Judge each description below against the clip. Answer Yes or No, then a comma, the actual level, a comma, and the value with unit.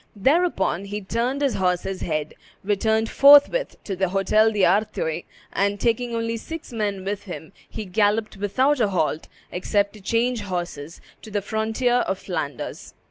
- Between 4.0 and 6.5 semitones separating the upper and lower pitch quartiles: No, average, 3.2 semitones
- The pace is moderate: Yes, average, 150 wpm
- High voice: Yes, high, 205 Hz